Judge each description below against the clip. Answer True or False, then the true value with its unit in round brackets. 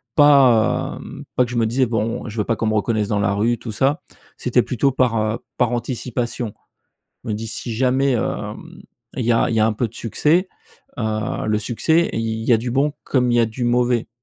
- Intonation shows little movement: True (2.3 semitones)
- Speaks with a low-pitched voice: True (120 Hz)